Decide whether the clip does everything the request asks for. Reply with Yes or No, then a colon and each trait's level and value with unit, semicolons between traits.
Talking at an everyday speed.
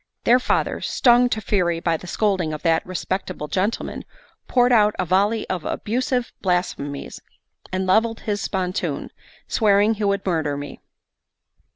Yes: average, 145 wpm